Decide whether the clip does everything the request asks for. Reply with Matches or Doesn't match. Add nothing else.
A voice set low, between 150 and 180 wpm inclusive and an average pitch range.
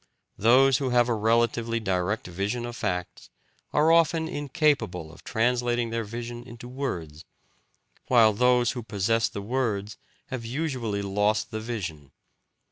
Doesn't match